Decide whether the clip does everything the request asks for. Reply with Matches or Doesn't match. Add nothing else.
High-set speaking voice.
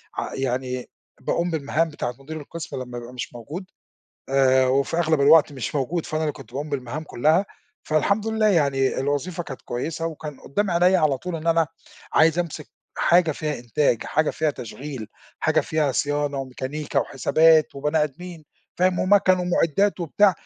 Doesn't match